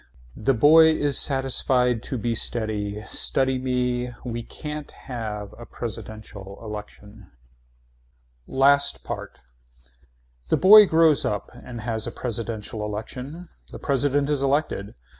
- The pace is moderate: No, slow, 120 wpm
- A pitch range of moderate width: Yes, average, 4.4 semitones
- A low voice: Yes, low, 125 Hz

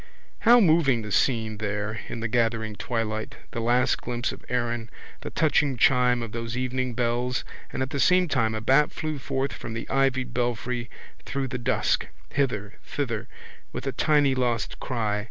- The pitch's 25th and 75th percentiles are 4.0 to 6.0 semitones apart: No, average, 2.9 semitones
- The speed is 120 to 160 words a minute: No, average, 170 wpm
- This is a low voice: Yes, low, 120 Hz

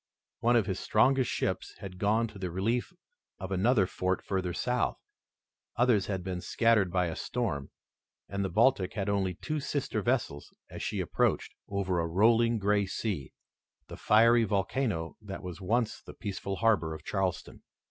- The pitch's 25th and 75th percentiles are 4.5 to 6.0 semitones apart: No, average, 3.8 semitones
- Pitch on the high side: No, low, 100 Hz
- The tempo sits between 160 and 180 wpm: Yes, average, 165 wpm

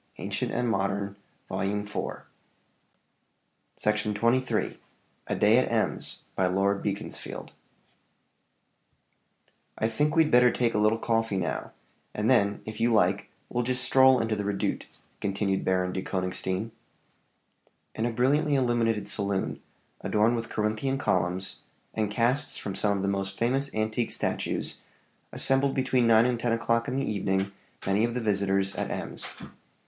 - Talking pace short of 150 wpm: Yes, average, 140 wpm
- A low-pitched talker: Yes, low, 110 Hz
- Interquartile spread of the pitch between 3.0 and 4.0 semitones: Yes, average, 3.4 semitones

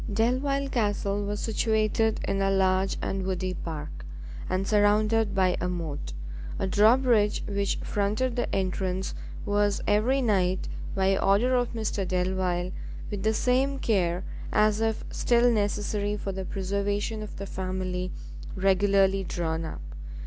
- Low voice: No, high, 200 Hz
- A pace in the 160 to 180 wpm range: No, slow, 135 wpm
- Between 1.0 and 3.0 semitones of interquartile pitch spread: Yes, narrow, 2.6 semitones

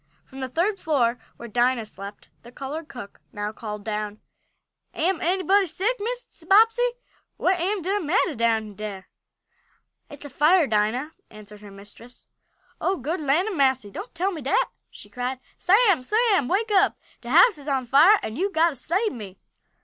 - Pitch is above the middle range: Yes, very high, 290 Hz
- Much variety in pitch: Yes, wide, 8.5 semitones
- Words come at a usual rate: Yes, average, 170 wpm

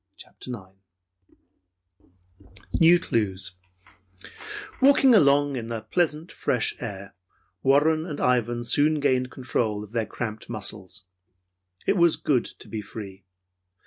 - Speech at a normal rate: No, slow, 115 wpm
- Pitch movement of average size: No, wide, 6.8 semitones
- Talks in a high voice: No, low, 115 Hz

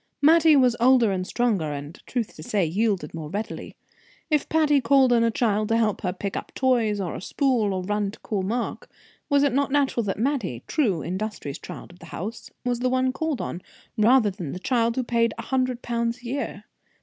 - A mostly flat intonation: No, average, 4.6 semitones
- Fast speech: Yes, fast, 215 wpm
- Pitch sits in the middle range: No, high, 230 Hz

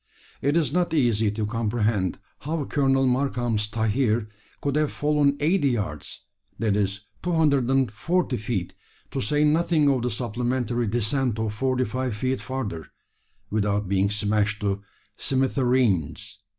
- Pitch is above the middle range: No, low, 120 Hz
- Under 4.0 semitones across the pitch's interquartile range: No, average, 4.6 semitones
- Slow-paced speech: Yes, slow, 130 wpm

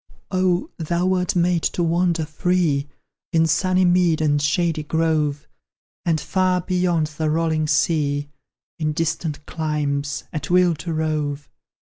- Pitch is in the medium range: Yes, medium, 160 Hz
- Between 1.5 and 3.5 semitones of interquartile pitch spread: Yes, average, 2.7 semitones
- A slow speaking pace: Yes, slow, 130 wpm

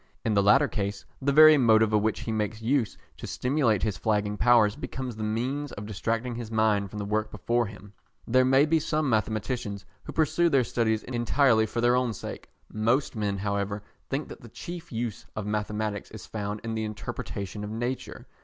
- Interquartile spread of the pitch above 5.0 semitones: No, average, 3.1 semitones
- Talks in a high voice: No, low, 110 Hz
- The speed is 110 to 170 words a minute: No, average, 195 wpm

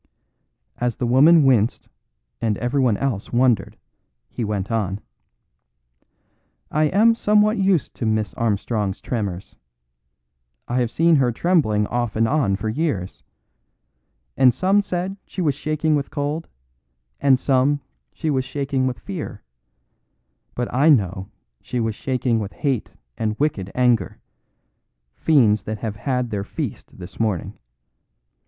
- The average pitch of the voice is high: No, low, 125 Hz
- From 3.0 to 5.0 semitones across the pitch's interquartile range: No, wide, 5.5 semitones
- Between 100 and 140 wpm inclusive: Yes, slow, 135 wpm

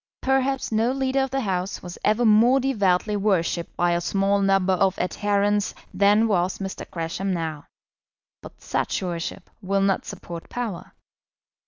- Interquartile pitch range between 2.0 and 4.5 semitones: Yes, average, 3.5 semitones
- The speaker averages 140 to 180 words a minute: Yes, average, 150 wpm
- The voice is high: Yes, high, 195 Hz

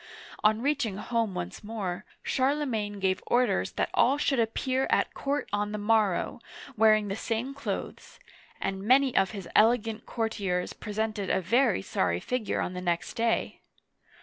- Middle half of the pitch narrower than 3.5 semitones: No, average, 3.9 semitones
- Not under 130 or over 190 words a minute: Yes, average, 150 wpm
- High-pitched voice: Yes, high, 215 Hz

